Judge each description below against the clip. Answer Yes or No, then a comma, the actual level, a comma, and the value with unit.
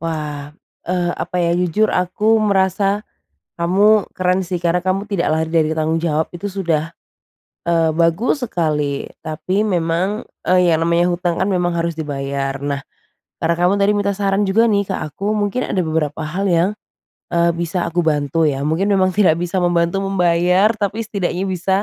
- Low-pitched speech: No, medium, 175 Hz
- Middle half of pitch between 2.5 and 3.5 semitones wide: Yes, average, 3.1 semitones